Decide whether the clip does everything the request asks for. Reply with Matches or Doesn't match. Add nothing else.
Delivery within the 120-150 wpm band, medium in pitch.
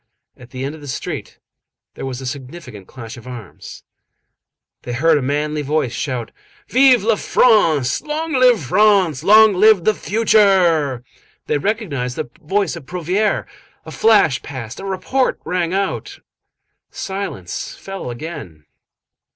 Matches